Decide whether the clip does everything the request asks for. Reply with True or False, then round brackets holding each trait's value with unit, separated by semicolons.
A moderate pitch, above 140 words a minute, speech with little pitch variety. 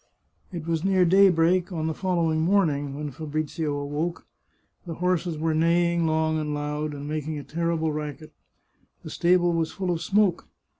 True (160 Hz; 160 wpm; 2.3 semitones)